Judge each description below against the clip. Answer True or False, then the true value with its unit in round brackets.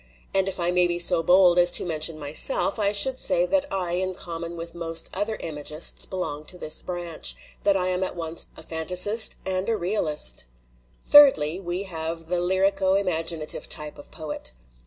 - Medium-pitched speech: True (175 Hz)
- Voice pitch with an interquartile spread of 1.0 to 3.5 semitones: True (2.6 semitones)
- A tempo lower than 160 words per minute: False (185 wpm)